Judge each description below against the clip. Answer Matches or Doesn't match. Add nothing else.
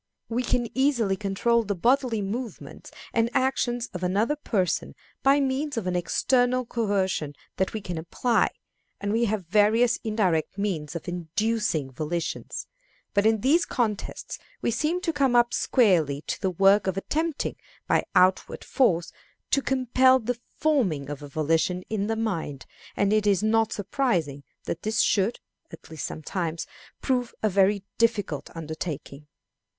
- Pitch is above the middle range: Matches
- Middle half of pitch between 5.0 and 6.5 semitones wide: Matches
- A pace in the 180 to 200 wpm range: Doesn't match